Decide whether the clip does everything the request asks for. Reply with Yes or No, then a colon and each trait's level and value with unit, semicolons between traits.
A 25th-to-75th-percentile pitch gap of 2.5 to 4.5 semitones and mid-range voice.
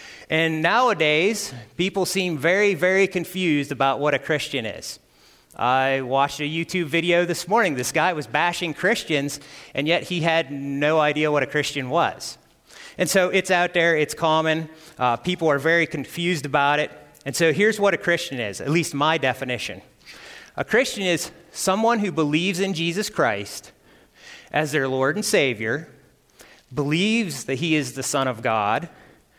Yes: average, 3.9 semitones; medium, 160 Hz